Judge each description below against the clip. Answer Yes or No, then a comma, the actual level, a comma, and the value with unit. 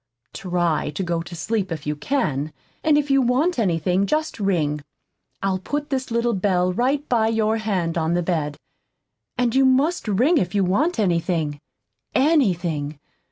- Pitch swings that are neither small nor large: No, wide, 7.3 semitones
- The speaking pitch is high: Yes, high, 195 Hz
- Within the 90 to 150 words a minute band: No, average, 160 wpm